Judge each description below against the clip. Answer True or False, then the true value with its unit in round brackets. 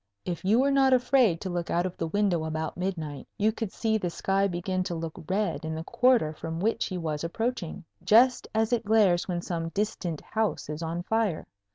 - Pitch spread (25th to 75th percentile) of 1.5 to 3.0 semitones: False (5.0 semitones)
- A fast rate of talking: True (210 wpm)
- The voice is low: False (185 Hz)